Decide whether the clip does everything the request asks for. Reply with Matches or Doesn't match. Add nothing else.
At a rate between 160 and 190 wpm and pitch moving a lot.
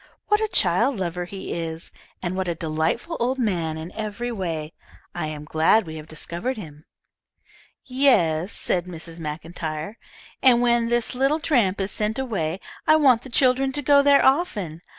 Matches